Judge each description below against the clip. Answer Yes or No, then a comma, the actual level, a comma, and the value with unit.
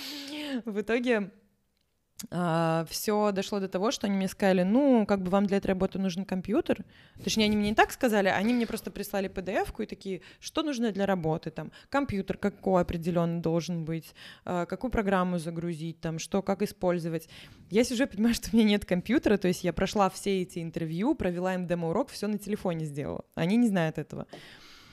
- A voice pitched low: No, high, 195 Hz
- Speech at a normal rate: No, fast, 185 wpm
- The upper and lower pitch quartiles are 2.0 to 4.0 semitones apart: Yes, average, 3.6 semitones